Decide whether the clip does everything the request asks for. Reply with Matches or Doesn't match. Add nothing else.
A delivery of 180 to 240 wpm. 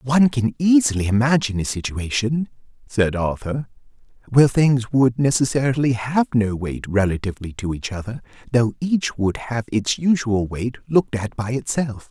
Doesn't match